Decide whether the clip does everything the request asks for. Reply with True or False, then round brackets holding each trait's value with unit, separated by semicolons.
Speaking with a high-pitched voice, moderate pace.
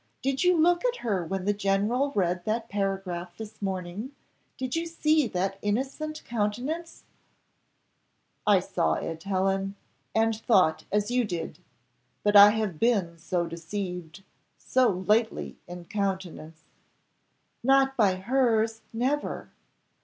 False (205 Hz; 125 wpm)